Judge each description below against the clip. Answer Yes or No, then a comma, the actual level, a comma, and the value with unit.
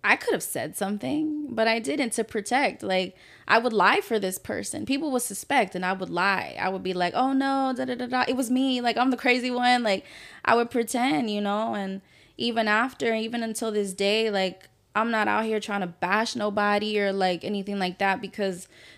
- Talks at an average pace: No, fast, 220 wpm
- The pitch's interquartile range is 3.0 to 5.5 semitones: Yes, average, 3.9 semitones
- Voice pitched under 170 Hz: No, high, 215 Hz